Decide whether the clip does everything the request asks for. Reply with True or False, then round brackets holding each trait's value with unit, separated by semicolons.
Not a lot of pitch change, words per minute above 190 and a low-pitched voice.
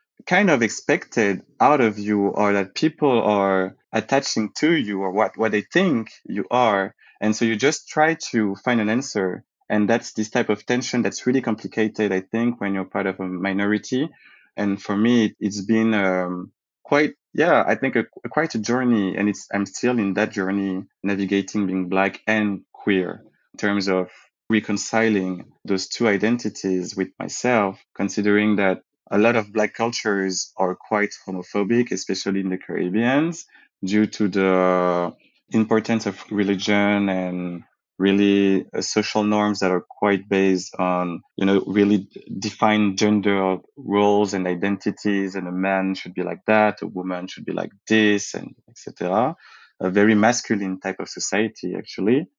False (2.3 semitones; 160 wpm; 100 Hz)